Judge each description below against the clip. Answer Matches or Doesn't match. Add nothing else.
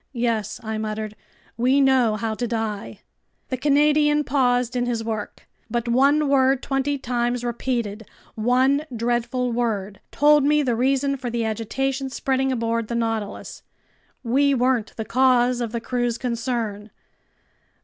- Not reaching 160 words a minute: Matches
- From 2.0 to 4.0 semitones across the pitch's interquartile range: Matches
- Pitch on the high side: Matches